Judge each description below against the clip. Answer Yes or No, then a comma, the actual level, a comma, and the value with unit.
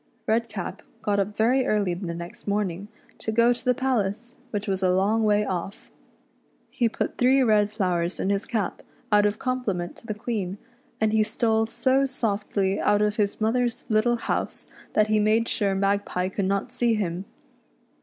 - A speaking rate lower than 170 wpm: No, average, 175 wpm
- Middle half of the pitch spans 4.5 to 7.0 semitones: No, average, 2.7 semitones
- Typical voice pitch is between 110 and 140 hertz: No, high, 210 Hz